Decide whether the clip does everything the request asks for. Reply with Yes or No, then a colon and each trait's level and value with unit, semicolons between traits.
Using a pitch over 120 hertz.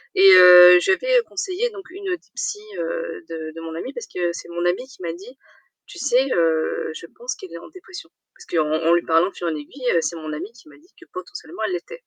Yes: high, 190 Hz